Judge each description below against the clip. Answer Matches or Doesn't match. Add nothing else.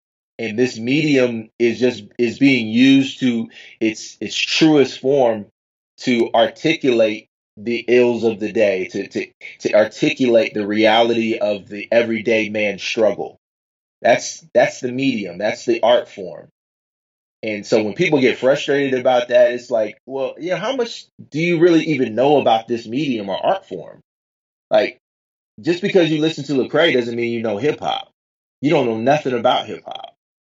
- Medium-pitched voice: Doesn't match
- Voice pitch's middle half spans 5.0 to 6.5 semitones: Doesn't match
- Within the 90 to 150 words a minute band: Doesn't match